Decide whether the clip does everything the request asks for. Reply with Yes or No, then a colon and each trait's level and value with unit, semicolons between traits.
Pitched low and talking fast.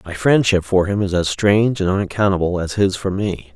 Yes: very low, 95 Hz; fast, 220 wpm